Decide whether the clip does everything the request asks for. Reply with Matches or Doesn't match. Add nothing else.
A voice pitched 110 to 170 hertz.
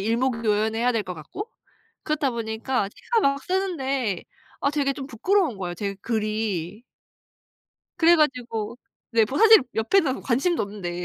Doesn't match